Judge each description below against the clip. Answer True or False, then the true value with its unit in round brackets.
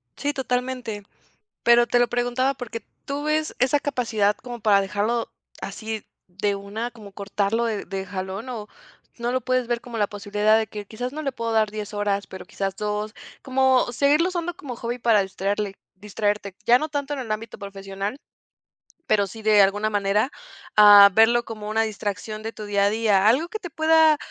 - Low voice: False (220 Hz)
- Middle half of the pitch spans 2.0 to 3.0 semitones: False (3.4 semitones)